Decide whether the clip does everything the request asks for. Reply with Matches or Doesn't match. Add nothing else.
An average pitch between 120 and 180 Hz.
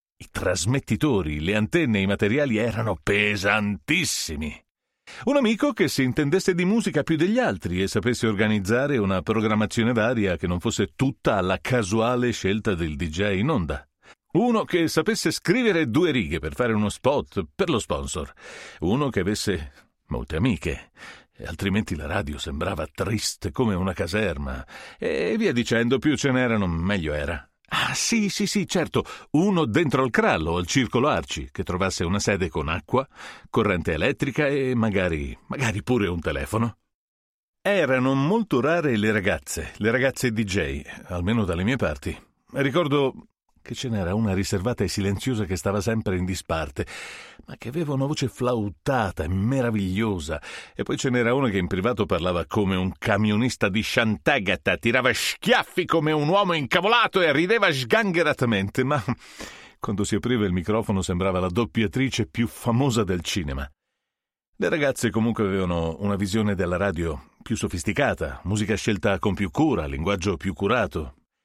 Doesn't match